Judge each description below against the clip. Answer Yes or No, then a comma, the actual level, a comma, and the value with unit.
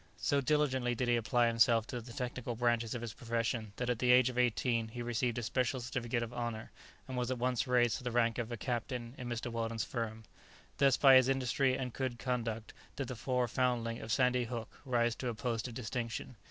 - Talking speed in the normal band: No, fast, 220 wpm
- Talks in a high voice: No, low, 120 Hz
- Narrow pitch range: Yes, narrow, 1.5 semitones